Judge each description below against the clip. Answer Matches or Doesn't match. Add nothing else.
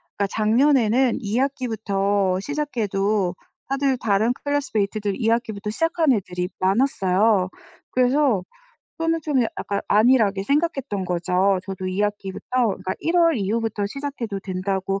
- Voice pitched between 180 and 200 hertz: Doesn't match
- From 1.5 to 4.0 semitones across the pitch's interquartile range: Doesn't match